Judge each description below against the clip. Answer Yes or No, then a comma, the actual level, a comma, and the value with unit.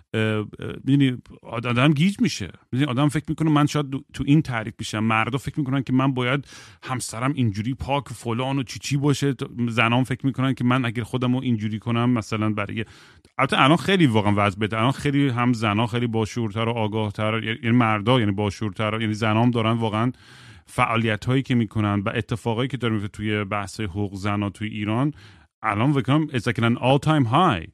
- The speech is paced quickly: Yes, fast, 165 wpm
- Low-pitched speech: Yes, low, 120 Hz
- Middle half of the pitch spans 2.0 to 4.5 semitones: Yes, average, 3.7 semitones